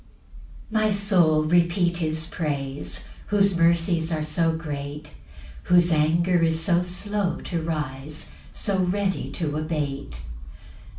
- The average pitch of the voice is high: No, medium, 165 Hz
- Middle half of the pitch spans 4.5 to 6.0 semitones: No, narrow, 2.6 semitones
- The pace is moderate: No, slow, 120 wpm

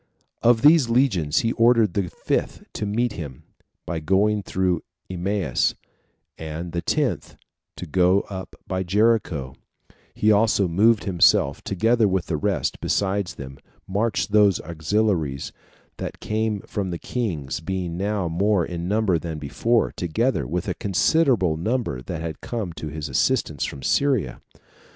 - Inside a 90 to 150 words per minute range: Yes, average, 140 wpm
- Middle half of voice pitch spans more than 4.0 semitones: Yes, average, 4.8 semitones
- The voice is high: No, very low, 95 Hz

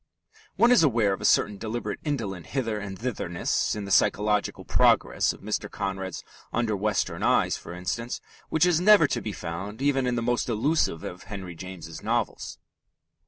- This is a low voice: Yes, low, 105 Hz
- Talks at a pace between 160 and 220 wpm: Yes, average, 170 wpm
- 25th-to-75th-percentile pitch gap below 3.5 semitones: No, average, 4.6 semitones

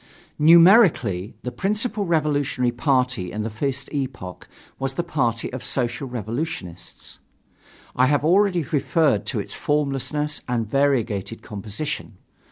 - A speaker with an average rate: No, slow, 120 wpm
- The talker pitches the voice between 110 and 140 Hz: Yes, low, 135 Hz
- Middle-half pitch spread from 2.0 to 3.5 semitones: No, average, 4.7 semitones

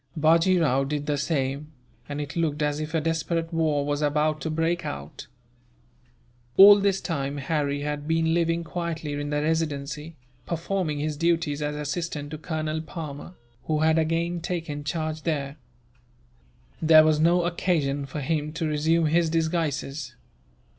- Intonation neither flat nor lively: No, narrow, 2.0 semitones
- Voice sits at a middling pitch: Yes, medium, 155 Hz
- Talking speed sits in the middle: Yes, average, 155 wpm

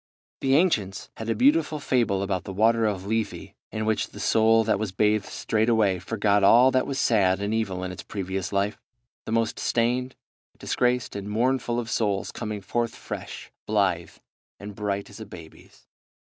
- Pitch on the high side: No, low, 110 Hz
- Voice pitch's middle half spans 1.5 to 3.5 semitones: Yes, average, 2.8 semitones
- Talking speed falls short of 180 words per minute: Yes, average, 170 wpm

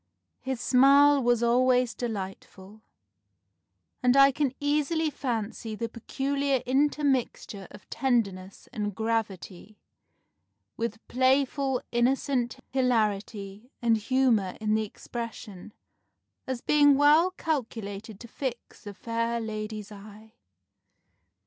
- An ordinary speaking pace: No, slow, 100 wpm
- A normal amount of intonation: Yes, average, 3.9 semitones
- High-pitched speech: Yes, high, 235 Hz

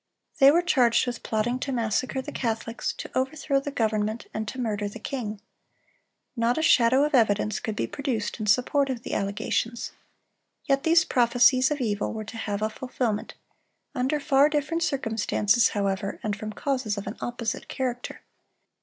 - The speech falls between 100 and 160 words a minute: No, average, 170 wpm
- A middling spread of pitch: Yes, average, 3.9 semitones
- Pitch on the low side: No, high, 240 Hz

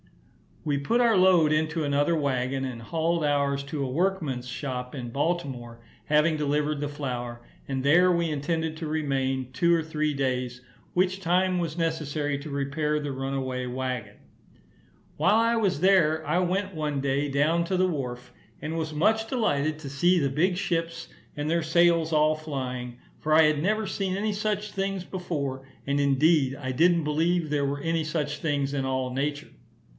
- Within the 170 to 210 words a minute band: Yes, average, 175 wpm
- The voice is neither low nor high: Yes, medium, 150 Hz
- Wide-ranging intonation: No, average, 3.7 semitones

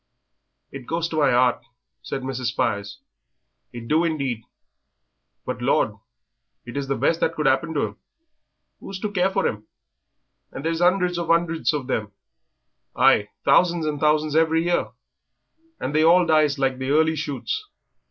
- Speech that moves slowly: No, average, 160 wpm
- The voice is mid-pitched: Yes, medium, 155 Hz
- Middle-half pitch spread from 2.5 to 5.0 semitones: Yes, average, 4.0 semitones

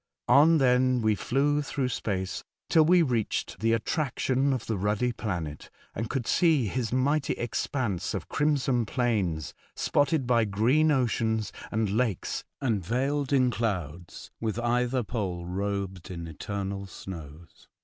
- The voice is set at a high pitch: No, low, 115 Hz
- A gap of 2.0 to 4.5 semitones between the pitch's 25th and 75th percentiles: No, average, 5.0 semitones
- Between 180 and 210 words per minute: No, average, 140 wpm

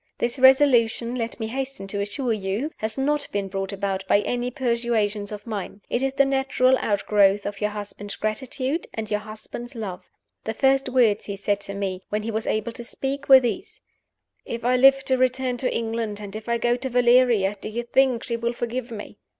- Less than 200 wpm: No, fast, 205 wpm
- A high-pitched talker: Yes, high, 235 Hz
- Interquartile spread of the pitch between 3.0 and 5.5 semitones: Yes, average, 3.7 semitones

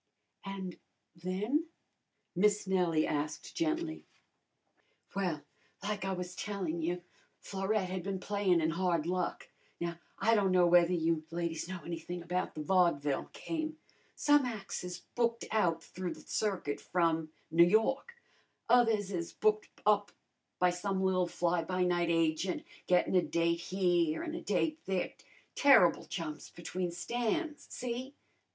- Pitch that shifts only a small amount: No, average, 3.5 semitones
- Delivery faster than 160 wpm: No, average, 140 wpm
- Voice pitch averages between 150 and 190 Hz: Yes, medium, 185 Hz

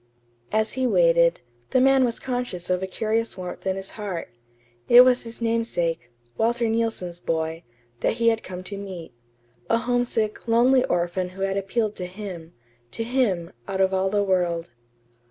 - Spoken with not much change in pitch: No, average, 4.4 semitones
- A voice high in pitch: Yes, high, 205 Hz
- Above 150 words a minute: Yes, average, 170 wpm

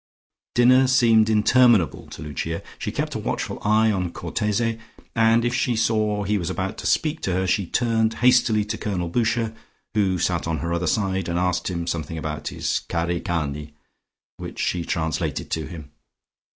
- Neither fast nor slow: Yes, average, 175 wpm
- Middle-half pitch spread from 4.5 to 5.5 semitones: Yes, average, 4.9 semitones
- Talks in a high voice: No, low, 100 Hz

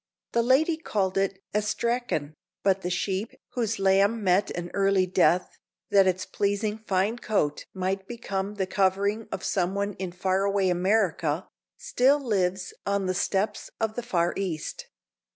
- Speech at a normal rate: Yes, average, 150 wpm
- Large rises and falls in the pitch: No, narrow, 2.4 semitones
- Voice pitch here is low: No, high, 195 Hz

